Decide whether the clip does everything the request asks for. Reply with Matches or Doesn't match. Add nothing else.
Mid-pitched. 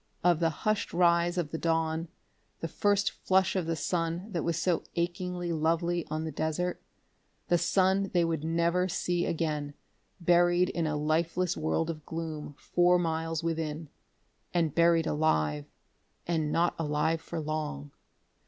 Matches